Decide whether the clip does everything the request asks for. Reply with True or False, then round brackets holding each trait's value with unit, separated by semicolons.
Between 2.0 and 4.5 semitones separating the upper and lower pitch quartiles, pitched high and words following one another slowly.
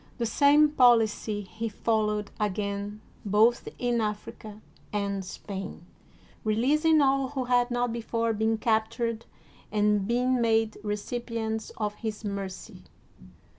True (2.5 semitones; 220 Hz; 120 wpm)